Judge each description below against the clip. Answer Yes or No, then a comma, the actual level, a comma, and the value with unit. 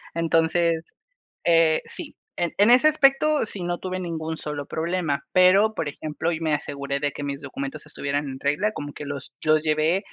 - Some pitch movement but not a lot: Yes, average, 3.9 semitones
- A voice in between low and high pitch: Yes, medium, 160 Hz